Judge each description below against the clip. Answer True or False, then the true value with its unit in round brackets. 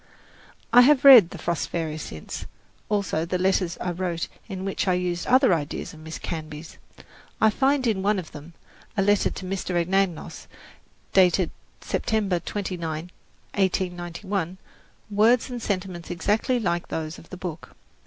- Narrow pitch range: False (3.2 semitones)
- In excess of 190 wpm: False (150 wpm)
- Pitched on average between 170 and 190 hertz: True (185 Hz)